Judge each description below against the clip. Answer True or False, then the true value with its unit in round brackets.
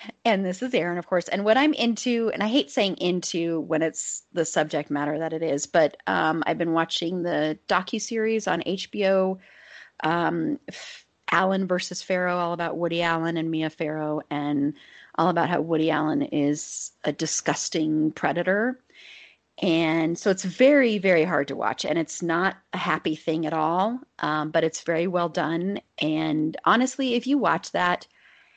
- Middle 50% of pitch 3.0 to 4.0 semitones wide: True (3.5 semitones)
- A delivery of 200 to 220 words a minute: False (175 wpm)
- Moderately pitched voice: True (170 Hz)